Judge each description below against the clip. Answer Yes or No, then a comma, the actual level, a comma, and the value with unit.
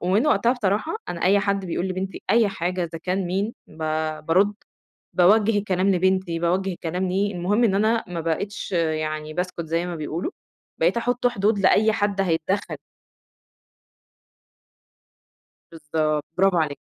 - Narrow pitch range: No, average, 3.2 semitones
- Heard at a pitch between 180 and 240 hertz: Yes, medium, 185 Hz